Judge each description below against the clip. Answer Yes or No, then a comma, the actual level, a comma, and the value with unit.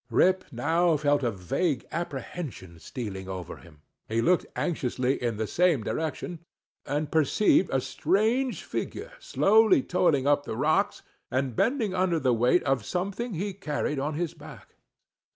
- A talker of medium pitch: Yes, medium, 150 Hz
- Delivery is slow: No, average, 150 wpm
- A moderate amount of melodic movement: No, wide, 6.4 semitones